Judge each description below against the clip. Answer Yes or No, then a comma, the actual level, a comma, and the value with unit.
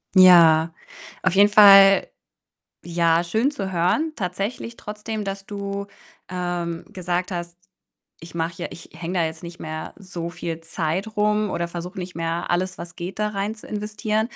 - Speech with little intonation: No, average, 3.3 semitones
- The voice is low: No, medium, 180 Hz